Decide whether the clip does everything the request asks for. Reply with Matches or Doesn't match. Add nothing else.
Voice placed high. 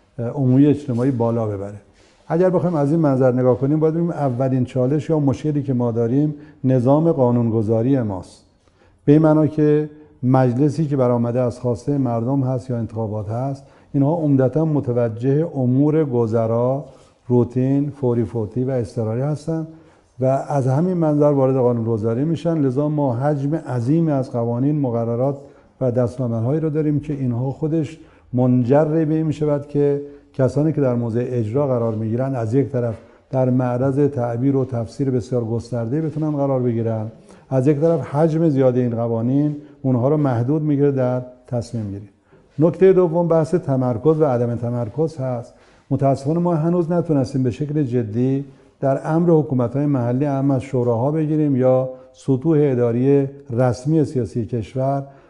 Doesn't match